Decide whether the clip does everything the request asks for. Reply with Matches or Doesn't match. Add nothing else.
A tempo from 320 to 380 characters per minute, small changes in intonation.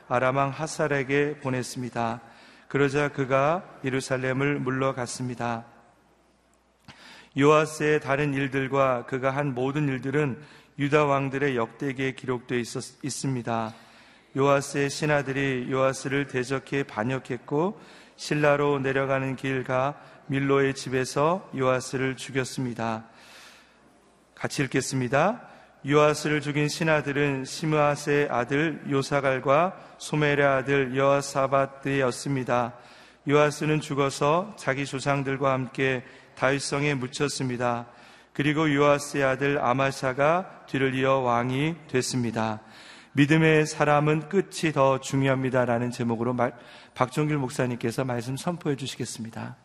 Doesn't match